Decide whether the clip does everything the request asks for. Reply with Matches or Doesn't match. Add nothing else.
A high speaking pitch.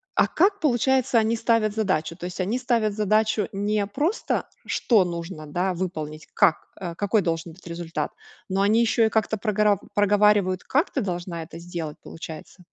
Matches